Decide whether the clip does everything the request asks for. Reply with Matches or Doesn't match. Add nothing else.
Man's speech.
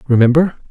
Matches